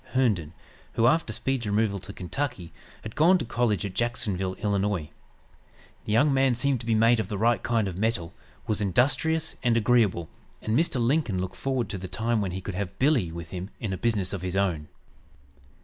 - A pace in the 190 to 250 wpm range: Yes, average, 195 wpm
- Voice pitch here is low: Yes, low, 110 Hz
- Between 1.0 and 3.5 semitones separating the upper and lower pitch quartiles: No, average, 4.5 semitones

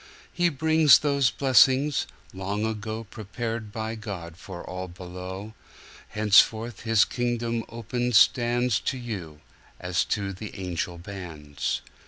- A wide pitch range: No, average, 4.3 semitones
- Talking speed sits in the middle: No, slow, 105 wpm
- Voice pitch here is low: Yes, low, 110 Hz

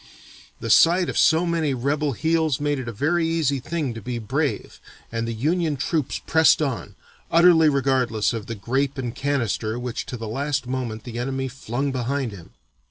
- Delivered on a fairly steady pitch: No, average, 4.5 semitones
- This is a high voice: No, low, 135 Hz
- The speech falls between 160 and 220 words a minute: Yes, average, 180 wpm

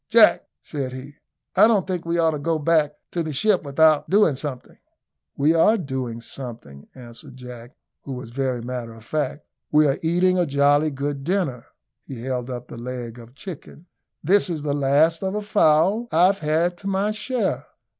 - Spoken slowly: No, average, 195 wpm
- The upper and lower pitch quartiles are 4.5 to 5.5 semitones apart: Yes, average, 5.1 semitones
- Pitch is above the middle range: No, medium, 145 Hz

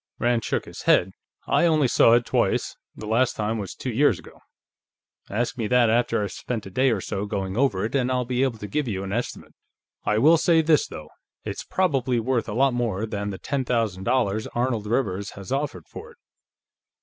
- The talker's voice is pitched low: Yes, low, 115 Hz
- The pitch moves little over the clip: No, average, 4.0 semitones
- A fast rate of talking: Yes, fast, 210 wpm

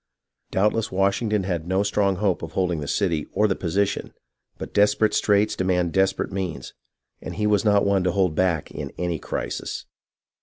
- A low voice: Yes, very low, 95 Hz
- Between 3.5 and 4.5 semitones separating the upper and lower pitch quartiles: No, narrow, 2.5 semitones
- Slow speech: No, average, 175 wpm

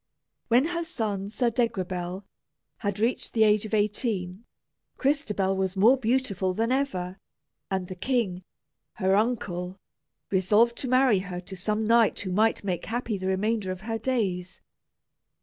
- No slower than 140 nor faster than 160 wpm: Yes, average, 150 wpm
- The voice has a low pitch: No, high, 210 Hz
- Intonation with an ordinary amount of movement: Yes, average, 3.8 semitones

